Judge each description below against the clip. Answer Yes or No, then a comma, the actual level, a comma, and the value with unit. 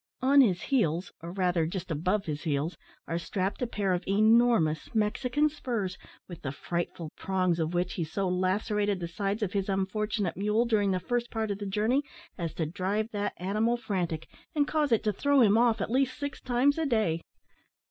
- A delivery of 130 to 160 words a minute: No, average, 195 wpm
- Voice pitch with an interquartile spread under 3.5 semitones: No, average, 4.6 semitones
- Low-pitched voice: No, high, 200 Hz